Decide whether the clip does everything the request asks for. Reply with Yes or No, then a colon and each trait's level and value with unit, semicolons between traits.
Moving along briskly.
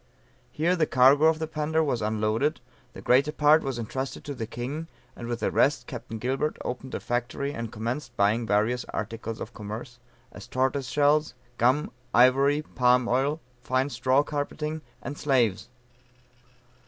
No: average, 155 wpm